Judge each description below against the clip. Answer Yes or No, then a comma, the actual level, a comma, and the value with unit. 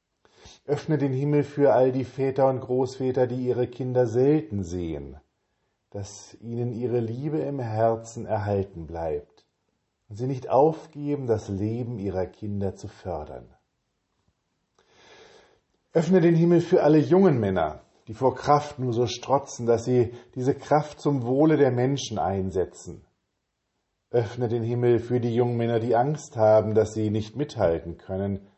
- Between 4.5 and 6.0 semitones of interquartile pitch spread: Yes, average, 5.2 semitones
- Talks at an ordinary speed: Yes, average, 145 wpm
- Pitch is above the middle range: No, low, 120 Hz